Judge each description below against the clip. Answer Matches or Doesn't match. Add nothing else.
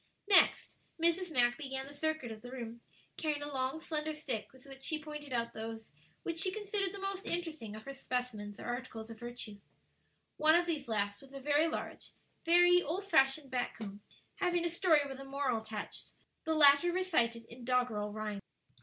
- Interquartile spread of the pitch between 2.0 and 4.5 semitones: Doesn't match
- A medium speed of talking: Matches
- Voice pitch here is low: Doesn't match